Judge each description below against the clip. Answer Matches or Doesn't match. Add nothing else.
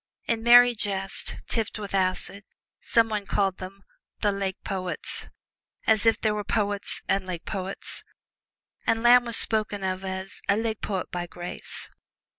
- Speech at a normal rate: Matches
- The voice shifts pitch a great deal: Doesn't match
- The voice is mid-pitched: Doesn't match